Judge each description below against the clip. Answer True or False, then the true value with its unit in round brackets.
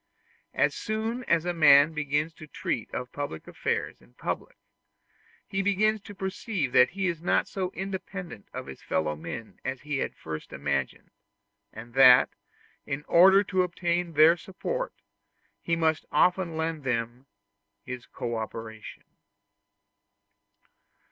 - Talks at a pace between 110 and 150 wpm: True (140 wpm)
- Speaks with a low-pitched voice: False (160 Hz)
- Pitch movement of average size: False (6.9 semitones)